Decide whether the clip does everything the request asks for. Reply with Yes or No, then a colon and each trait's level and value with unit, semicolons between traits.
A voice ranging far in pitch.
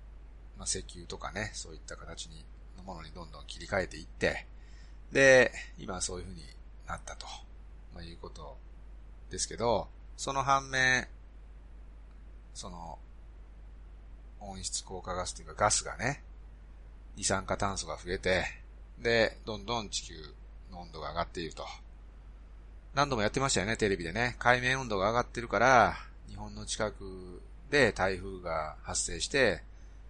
Yes: wide, 6.2 semitones